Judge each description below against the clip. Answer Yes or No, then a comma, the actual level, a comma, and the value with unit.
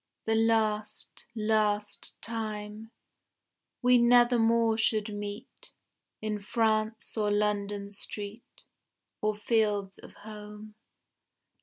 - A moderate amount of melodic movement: No, narrow, 1.3 semitones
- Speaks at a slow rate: Yes, slow, 90 wpm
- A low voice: No, high, 215 Hz